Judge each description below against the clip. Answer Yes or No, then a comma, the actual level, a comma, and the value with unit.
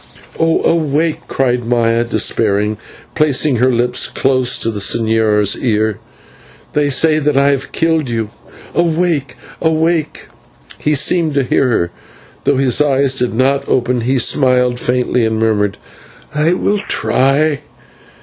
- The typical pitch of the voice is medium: No, low, 130 Hz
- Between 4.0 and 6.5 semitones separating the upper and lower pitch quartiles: Yes, average, 4.4 semitones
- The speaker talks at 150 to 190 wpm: No, average, 140 wpm